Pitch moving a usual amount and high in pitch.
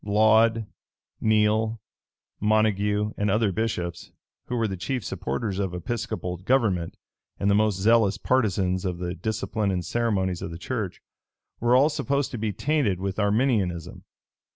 No: average, 3.2 semitones; low, 105 Hz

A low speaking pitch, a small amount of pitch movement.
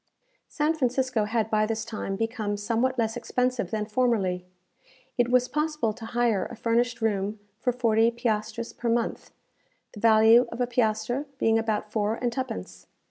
No: high, 230 Hz; narrow, 2.2 semitones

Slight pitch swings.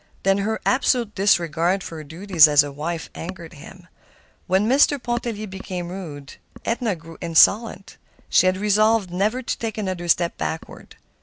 No: average, 4.2 semitones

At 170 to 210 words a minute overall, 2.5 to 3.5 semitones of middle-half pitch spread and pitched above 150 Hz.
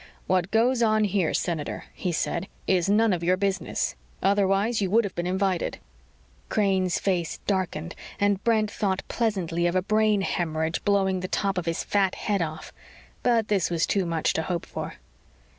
Yes: average, 175 wpm; average, 2.9 semitones; high, 190 Hz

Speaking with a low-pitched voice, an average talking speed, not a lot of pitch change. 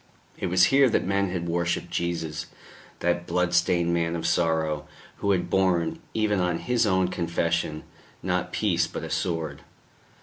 Yes: very low, 85 Hz; average, 160 wpm; narrow, 1.8 semitones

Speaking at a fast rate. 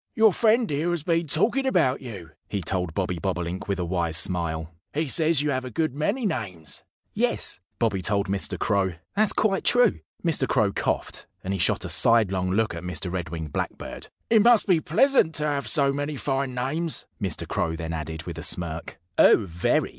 No: average, 195 wpm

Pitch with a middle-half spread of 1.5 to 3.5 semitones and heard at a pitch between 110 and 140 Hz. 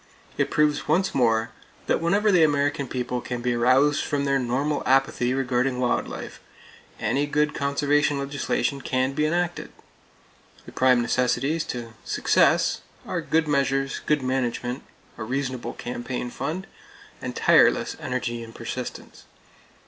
Yes: average, 2.9 semitones; low, 135 Hz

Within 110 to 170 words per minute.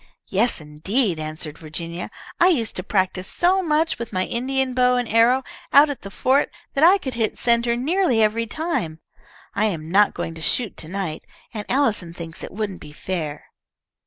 No: average, 185 wpm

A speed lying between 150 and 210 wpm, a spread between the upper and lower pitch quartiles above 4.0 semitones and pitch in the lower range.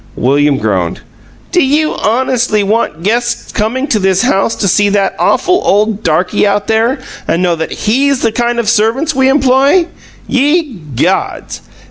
No: average, 155 wpm; average, 5.0 semitones; high, 225 Hz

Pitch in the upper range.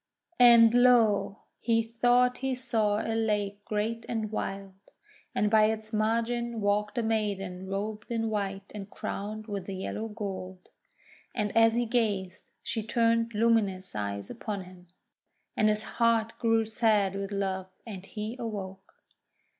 Yes: high, 215 Hz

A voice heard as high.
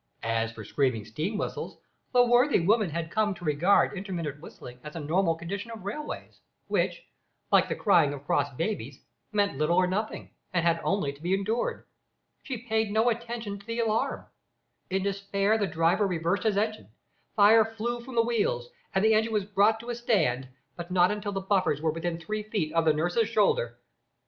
Yes: high, 195 Hz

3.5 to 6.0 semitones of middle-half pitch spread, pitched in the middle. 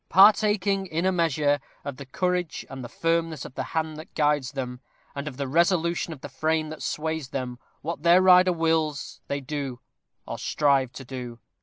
Yes: average, 3.8 semitones; medium, 155 Hz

